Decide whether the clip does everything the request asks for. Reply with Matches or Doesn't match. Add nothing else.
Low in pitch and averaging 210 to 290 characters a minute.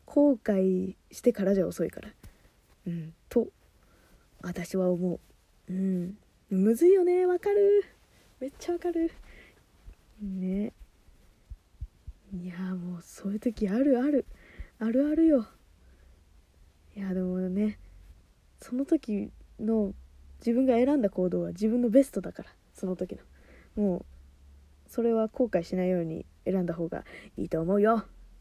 Doesn't match